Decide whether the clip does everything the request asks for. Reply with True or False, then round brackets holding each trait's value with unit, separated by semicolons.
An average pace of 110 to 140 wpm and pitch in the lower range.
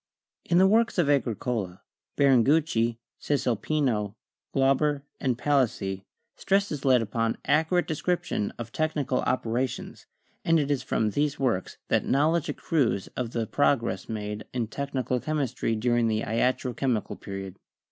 True (135 wpm; 130 Hz)